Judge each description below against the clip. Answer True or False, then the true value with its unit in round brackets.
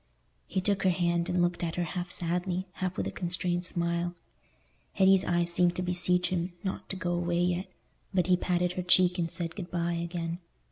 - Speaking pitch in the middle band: True (175 Hz)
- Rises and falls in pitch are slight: True (0.9 semitones)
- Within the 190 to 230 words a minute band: True (200 wpm)